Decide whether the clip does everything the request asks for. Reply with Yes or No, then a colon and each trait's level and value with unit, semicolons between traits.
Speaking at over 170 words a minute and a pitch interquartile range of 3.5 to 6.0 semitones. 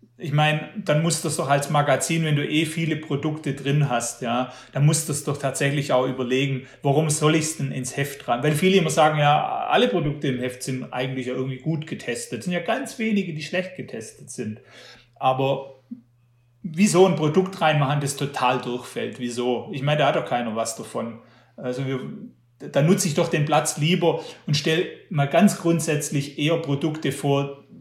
Yes: fast, 190 wpm; average, 3.9 semitones